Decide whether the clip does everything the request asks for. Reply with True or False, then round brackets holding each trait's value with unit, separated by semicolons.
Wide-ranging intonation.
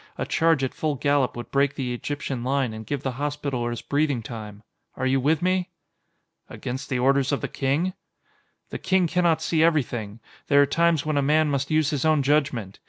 False (3.4 semitones)